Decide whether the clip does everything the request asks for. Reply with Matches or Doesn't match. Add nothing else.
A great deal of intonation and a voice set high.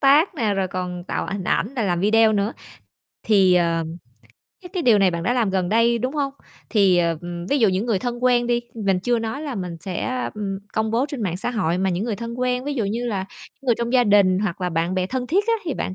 Doesn't match